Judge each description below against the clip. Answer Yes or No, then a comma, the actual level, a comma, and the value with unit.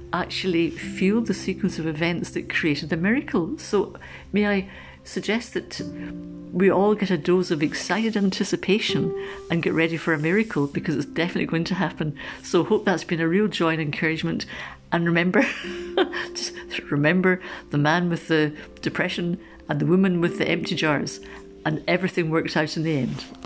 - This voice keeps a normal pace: Yes, average, 170 wpm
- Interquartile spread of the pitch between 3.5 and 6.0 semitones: No, average, 3.1 semitones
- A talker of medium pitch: Yes, medium, 175 Hz